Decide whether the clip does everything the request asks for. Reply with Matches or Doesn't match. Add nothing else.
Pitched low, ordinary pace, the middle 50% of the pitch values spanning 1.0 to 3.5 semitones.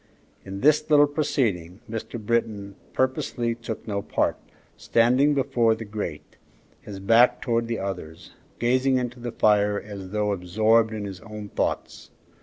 Matches